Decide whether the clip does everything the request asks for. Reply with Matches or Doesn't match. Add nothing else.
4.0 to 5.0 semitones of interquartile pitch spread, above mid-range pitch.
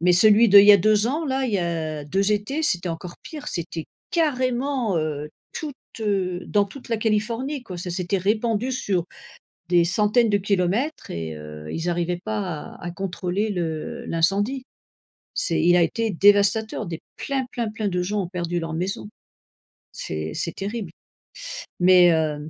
Matches